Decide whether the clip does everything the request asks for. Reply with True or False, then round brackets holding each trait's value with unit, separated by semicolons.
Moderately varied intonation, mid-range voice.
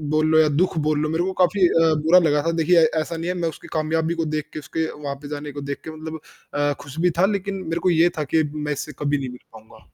False (2.2 semitones; 160 Hz)